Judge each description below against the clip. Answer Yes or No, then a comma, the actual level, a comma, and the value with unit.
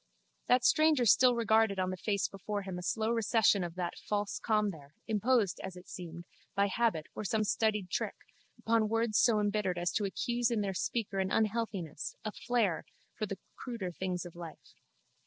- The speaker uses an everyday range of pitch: Yes, average, 3.6 semitones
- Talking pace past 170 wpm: Yes, average, 185 wpm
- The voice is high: Yes, high, 205 Hz